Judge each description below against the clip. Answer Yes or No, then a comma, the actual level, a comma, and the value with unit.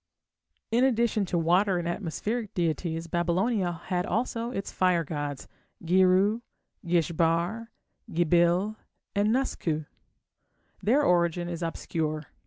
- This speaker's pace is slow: Yes, slow, 110 wpm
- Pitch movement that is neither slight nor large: Yes, average, 3.9 semitones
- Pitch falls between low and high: Yes, medium, 175 Hz